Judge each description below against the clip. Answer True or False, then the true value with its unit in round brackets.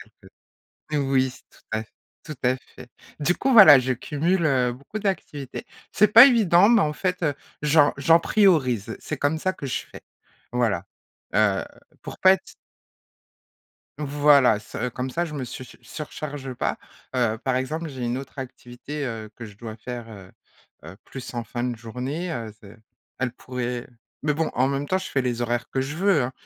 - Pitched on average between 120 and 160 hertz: True (135 Hz)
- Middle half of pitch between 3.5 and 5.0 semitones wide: True (4.2 semitones)